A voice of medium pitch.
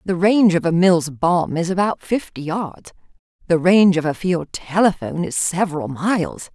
Yes: medium, 175 Hz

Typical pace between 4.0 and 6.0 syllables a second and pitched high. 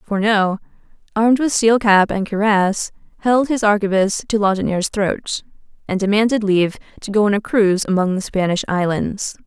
Yes: 5.4 syllables/s; high, 205 Hz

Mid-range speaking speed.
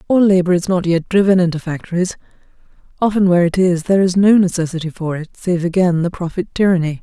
Yes: average, 195 wpm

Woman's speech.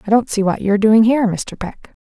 Yes: female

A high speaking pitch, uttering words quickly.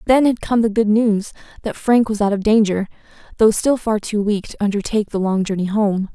Yes: high, 210 Hz; fast, 225 wpm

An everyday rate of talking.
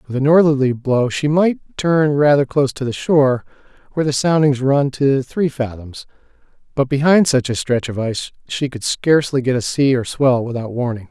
Yes: average, 195 wpm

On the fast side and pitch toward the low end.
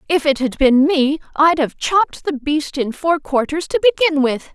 No: fast, 210 wpm; very high, 300 Hz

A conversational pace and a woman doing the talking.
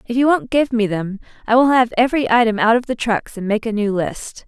No: fast, 270 wpm; female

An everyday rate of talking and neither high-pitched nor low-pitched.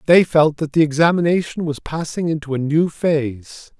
Yes: average, 175 wpm; medium, 155 Hz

